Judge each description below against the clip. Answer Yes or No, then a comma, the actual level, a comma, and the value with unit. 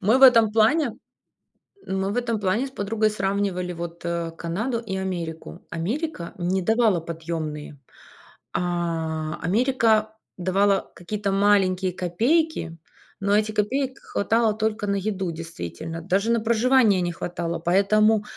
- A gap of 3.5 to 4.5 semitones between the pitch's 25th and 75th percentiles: Yes, average, 4.2 semitones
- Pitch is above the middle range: Yes, high, 195 Hz